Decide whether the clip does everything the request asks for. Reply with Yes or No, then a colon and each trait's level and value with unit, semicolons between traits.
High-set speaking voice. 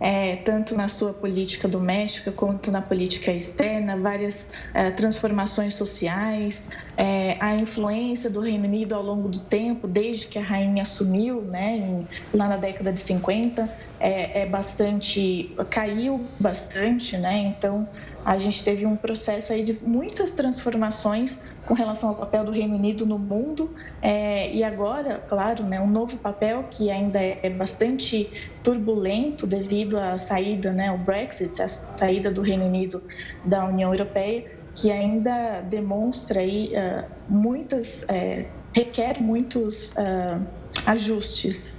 Yes: high, 205 Hz